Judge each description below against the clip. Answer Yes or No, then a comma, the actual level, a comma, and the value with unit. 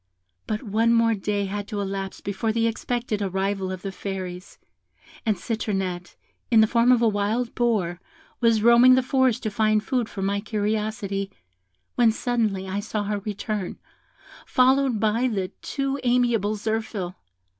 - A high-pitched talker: Yes, high, 215 Hz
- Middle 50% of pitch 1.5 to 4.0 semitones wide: Yes, average, 2.8 semitones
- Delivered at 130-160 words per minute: Yes, average, 155 wpm